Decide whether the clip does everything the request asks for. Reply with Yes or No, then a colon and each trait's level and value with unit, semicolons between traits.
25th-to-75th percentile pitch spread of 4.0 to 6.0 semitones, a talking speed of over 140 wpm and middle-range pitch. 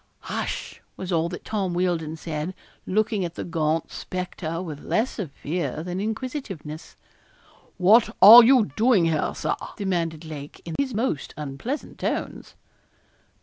No: average, 5.2 semitones; slow, 135 wpm; medium, 180 Hz